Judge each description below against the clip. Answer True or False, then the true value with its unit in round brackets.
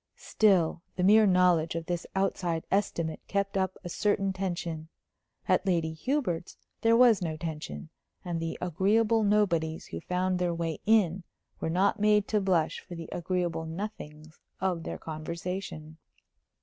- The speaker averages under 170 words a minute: True (150 wpm)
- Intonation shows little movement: False (3.3 semitones)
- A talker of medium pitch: True (180 Hz)